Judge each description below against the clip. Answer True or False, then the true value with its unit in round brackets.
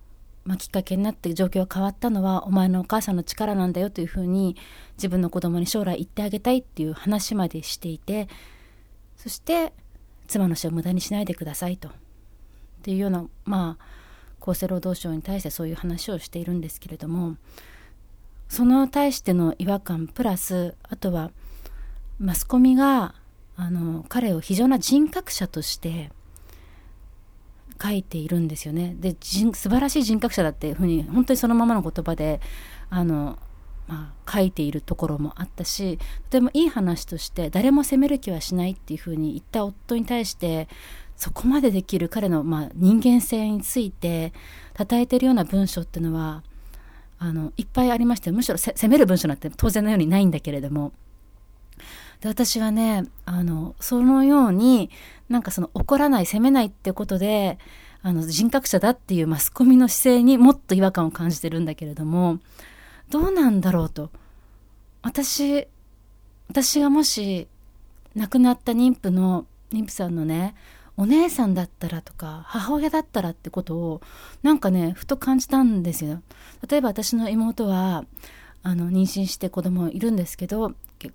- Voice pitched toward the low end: False (185 Hz)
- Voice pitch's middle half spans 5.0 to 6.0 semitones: True (5.7 semitones)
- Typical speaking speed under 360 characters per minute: True (330 characters per minute)